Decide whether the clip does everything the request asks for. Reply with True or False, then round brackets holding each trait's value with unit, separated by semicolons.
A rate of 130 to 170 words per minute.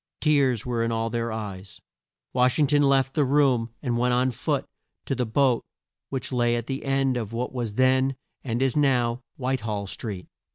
False (195 wpm)